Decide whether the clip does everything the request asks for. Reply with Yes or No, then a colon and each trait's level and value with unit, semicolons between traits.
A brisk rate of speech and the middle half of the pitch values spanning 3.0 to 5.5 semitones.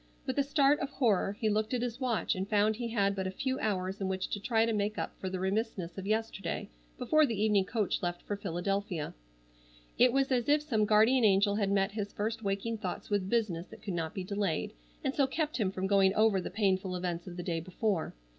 Yes: fast, 230 wpm; average, 3.3 semitones